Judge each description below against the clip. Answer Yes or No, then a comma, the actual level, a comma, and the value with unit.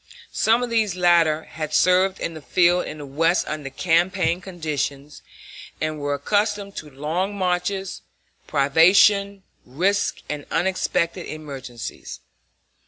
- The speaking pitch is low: No, medium, 170 Hz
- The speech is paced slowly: Yes, slow, 120 wpm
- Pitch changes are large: No, average, 4.0 semitones